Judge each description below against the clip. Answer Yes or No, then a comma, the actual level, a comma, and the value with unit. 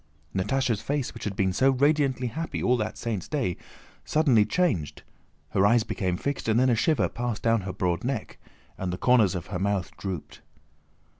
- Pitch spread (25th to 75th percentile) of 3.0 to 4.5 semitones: No, wide, 5.5 semitones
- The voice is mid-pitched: No, low, 115 Hz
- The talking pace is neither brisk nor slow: Yes, average, 180 wpm